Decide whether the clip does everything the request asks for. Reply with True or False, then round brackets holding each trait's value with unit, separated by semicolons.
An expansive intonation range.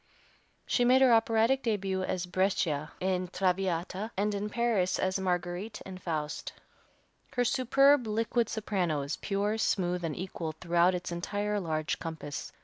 False (3.9 semitones)